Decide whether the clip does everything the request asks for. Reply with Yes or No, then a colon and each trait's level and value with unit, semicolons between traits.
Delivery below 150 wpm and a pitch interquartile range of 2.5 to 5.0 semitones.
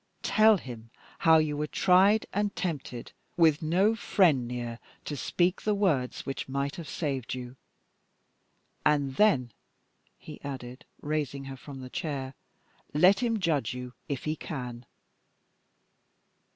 No: slow, 135 wpm; wide, 5.6 semitones